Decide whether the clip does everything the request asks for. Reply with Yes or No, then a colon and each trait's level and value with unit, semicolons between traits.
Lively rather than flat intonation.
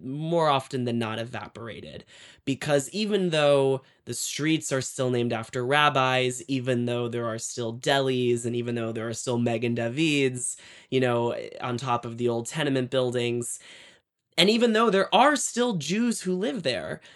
No: average, 4.0 semitones